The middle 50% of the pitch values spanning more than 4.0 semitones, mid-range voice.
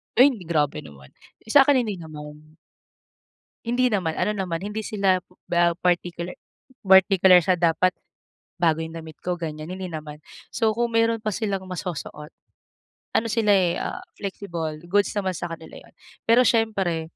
Yes: average, 4.5 semitones; medium, 180 Hz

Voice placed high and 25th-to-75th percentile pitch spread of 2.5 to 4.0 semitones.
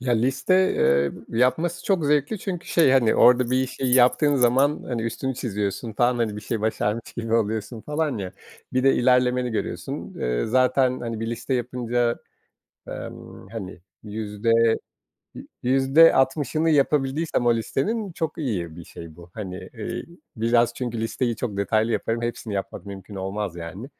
No: low, 120 Hz; average, 3.6 semitones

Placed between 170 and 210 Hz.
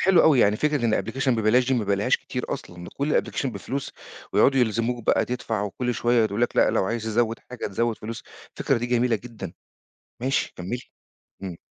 No: low, 115 Hz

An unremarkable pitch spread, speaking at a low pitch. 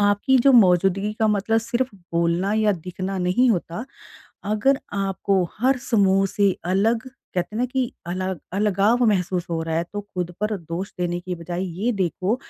No: average, 3.3 semitones; high, 195 Hz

